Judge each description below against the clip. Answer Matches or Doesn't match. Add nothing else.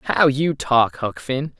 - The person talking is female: Doesn't match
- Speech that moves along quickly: Doesn't match